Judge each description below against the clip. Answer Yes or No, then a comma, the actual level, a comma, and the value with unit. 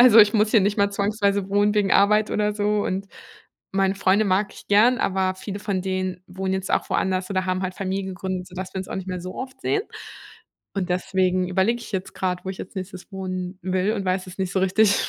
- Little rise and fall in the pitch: Yes, narrow, 1.7 semitones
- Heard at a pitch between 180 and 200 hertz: Yes, high, 190 Hz